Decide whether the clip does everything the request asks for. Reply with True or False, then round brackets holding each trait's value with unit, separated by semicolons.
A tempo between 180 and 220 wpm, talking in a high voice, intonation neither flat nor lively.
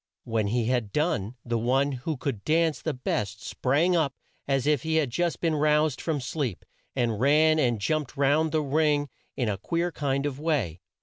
False (190 wpm; 140 Hz; 4.2 semitones)